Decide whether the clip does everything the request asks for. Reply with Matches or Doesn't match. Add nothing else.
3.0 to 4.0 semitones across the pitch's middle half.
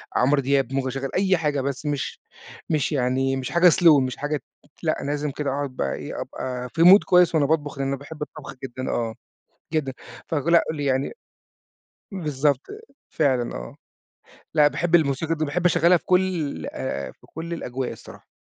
Matches